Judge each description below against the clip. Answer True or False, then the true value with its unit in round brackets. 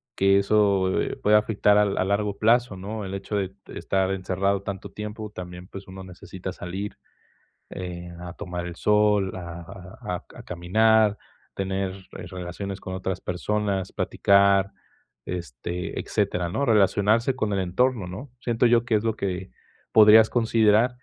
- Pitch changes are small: True (2.3 semitones)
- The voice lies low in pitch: True (100 Hz)